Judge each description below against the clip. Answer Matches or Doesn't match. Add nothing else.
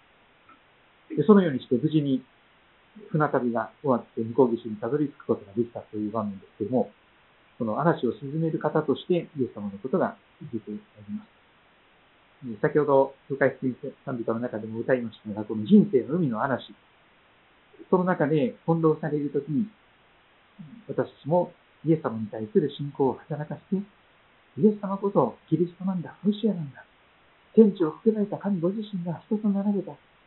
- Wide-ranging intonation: Matches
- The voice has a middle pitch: Matches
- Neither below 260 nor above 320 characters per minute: Doesn't match